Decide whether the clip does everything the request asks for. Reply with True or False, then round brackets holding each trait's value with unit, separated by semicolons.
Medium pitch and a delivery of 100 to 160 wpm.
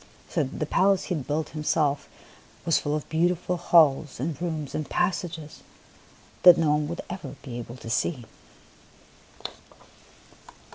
True (155 Hz; 140 wpm)